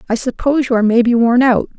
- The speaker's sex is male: No, female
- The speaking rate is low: No, fast, 235 wpm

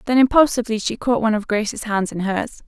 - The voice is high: Yes, high, 225 Hz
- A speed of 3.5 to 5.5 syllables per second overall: No, 6.4 syllables/s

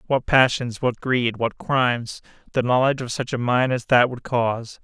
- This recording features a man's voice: Yes, male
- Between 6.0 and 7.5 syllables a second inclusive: No, 4.8 syllables/s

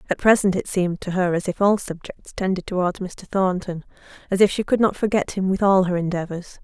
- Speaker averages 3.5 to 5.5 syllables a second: No, 5.7 syllables/s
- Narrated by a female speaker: Yes, female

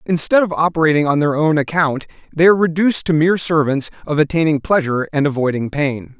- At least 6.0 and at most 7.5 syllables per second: Yes, 6.2 syllables/s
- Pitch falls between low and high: Yes, medium, 155 Hz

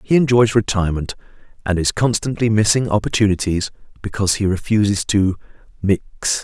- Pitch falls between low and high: No, low, 105 Hz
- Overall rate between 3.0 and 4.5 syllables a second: No, 5.5 syllables/s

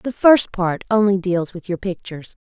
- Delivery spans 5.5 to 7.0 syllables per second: No, 4.9 syllables/s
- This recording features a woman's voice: Yes, female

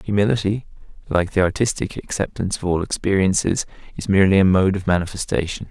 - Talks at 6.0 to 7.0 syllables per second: Yes, 6.4 syllables/s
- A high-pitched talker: No, very low, 95 Hz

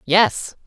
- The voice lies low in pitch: No, high, 190 Hz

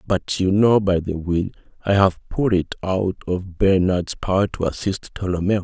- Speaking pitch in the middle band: No, very low, 95 Hz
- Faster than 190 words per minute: No, average, 180 wpm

